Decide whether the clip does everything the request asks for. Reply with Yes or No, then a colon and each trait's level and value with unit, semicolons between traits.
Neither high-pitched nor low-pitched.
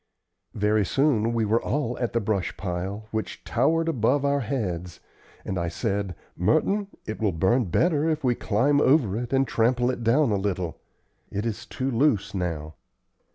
No: low, 115 Hz